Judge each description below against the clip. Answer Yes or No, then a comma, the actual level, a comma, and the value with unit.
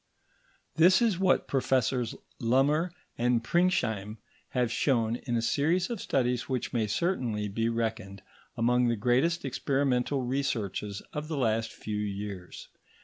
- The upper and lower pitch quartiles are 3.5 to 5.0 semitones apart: Yes, average, 4.1 semitones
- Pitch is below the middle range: Yes, low, 125 Hz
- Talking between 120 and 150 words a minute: Yes, slow, 135 wpm